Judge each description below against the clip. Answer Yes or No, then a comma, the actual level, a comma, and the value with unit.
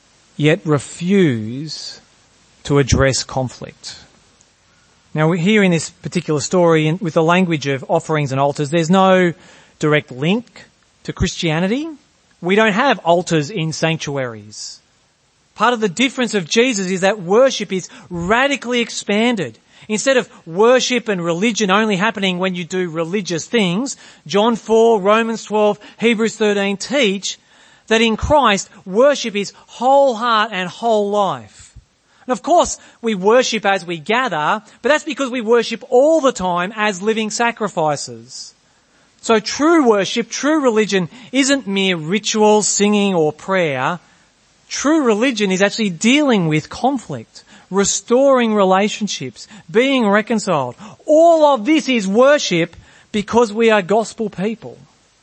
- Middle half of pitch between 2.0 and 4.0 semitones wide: No, average, 5.3 semitones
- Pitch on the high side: Yes, high, 210 Hz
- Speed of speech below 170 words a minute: Yes, slow, 135 wpm